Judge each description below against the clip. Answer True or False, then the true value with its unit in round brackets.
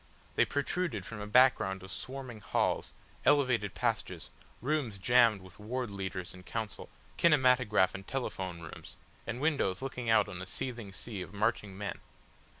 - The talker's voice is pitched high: False (110 Hz)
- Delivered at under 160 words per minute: True (150 wpm)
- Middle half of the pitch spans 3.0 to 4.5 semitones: False (5.0 semitones)